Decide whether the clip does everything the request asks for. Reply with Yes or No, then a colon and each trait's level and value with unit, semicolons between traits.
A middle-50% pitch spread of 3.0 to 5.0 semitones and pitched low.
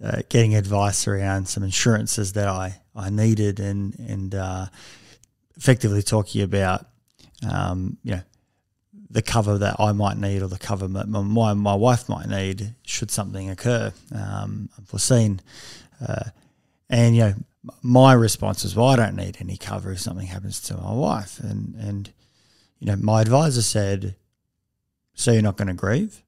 No: narrow, 2.5 semitones; low, 105 Hz